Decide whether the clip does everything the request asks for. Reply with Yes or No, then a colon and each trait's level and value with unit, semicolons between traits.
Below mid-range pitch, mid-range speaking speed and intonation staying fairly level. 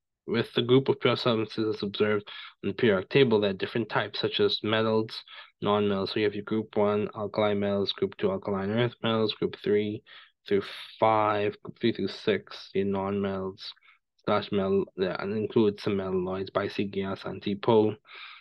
Yes: low, 105 Hz; average, 180 wpm; narrow, 1.6 semitones